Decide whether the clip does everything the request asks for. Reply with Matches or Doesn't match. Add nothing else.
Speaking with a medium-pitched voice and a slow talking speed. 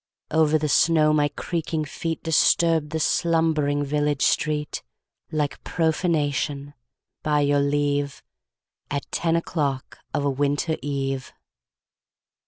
Matches